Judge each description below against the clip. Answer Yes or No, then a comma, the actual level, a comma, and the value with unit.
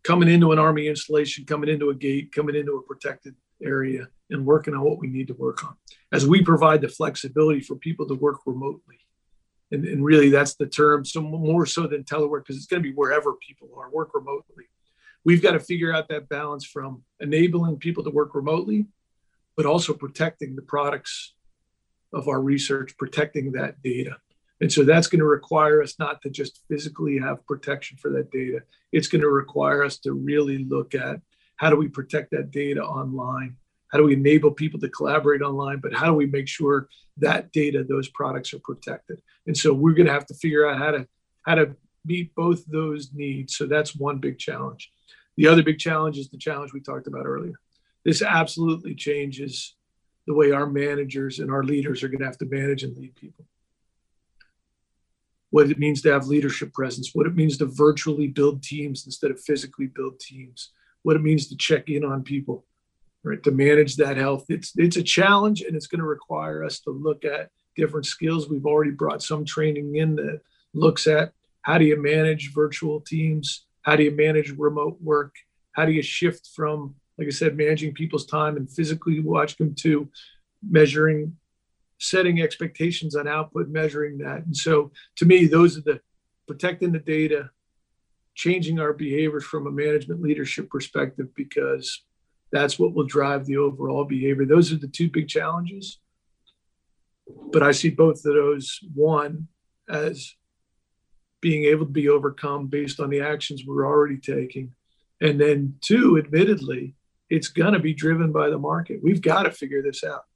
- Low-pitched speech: No, medium, 150 Hz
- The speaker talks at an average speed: Yes, average, 185 wpm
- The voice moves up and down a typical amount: No, narrow, 2.0 semitones